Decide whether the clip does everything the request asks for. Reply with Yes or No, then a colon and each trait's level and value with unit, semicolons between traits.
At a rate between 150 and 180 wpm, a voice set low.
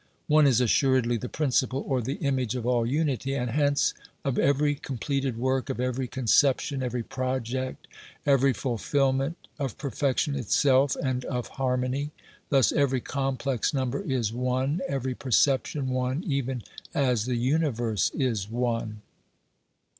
No: slow, 135 wpm; low, 130 Hz